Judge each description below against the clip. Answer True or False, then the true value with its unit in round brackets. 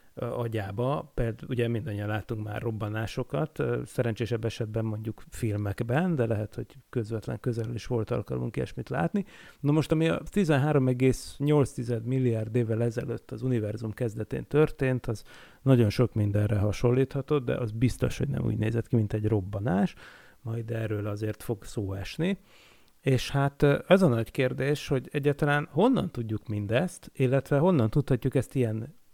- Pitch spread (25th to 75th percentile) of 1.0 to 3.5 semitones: False (4.0 semitones)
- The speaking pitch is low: True (120 Hz)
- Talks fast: False (145 wpm)